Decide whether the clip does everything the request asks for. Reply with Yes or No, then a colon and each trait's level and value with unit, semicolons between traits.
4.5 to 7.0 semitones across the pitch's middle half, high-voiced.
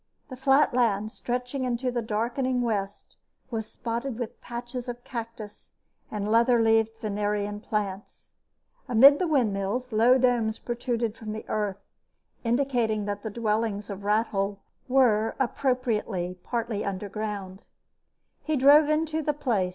No: average, 3.1 semitones; high, 230 Hz